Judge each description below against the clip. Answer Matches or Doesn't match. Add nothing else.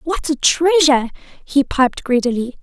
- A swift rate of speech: Doesn't match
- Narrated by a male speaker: Doesn't match